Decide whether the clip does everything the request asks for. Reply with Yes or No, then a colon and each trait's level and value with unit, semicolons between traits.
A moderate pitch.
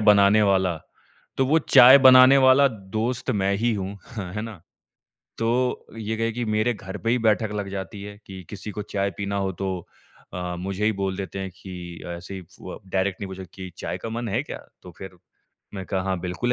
No: low, 100 Hz